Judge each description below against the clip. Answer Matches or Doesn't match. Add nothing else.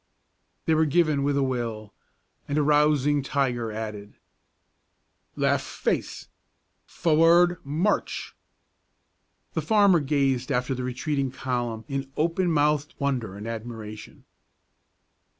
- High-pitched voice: Doesn't match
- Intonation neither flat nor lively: Matches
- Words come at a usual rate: Doesn't match